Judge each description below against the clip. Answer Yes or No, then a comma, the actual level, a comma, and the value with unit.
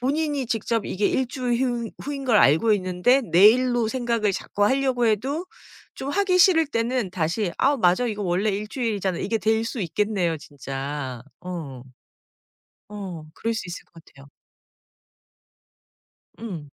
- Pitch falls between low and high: No, high, 220 Hz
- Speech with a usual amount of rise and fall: No, wide, 5.8 semitones